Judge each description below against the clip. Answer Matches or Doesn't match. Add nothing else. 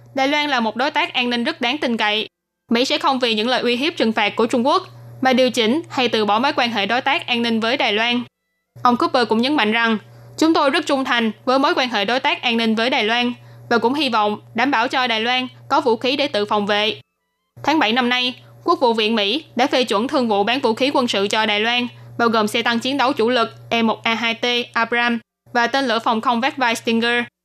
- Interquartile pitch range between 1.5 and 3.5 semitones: Matches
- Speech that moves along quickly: Matches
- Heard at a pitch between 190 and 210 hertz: Doesn't match